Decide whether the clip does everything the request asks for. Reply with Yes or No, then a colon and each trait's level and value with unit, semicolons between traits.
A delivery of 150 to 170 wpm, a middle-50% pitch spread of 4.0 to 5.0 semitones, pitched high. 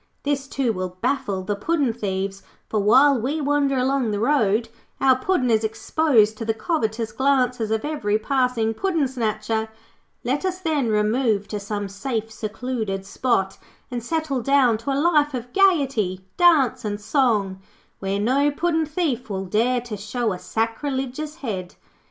Yes: average, 155 wpm; average, 4.7 semitones; high, 240 Hz